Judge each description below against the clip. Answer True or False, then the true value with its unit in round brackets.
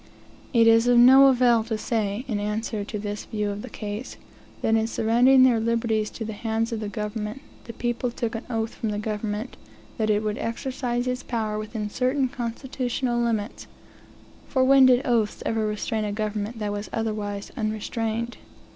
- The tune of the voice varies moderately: False (2.3 semitones)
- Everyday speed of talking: True (180 wpm)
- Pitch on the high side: True (225 Hz)